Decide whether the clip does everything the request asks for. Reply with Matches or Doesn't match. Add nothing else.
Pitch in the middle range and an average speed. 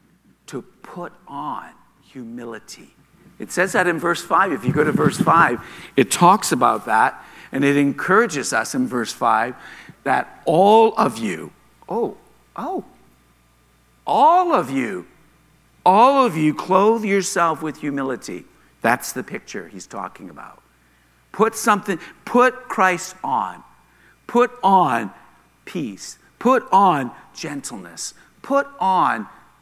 Doesn't match